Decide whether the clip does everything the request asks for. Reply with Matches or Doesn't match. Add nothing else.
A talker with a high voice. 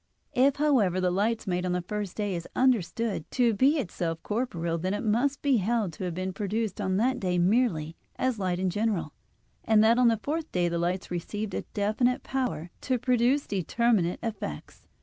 Matches